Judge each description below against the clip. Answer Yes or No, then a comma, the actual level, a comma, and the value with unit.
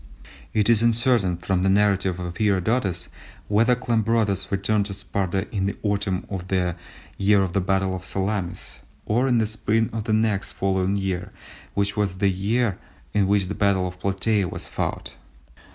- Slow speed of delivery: No, average, 170 wpm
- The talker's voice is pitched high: No, low, 100 Hz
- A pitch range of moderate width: No, narrow, 2.3 semitones